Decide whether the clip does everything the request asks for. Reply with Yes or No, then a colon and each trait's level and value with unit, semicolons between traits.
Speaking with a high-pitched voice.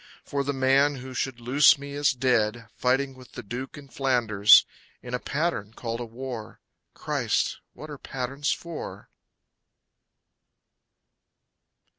No: low, 130 Hz